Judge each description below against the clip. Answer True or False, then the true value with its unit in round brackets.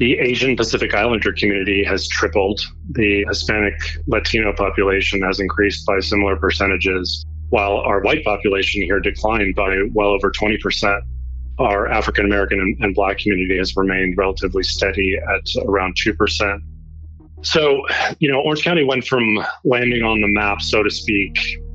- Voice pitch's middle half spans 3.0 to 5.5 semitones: False (2.6 semitones)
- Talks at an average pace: True (150 wpm)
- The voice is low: True (100 Hz)